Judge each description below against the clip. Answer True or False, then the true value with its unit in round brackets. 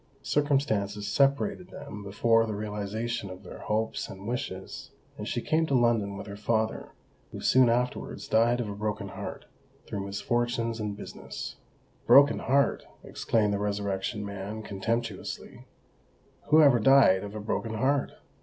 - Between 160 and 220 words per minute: False (145 wpm)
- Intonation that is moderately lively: True (3.1 semitones)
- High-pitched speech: False (110 Hz)